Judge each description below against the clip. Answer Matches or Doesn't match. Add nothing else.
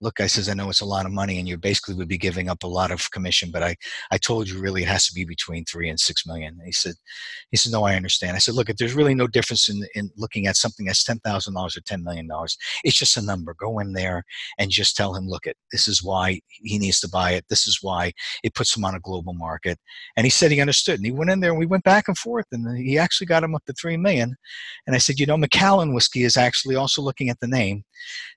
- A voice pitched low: Matches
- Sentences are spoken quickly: Matches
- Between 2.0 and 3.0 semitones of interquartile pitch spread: Doesn't match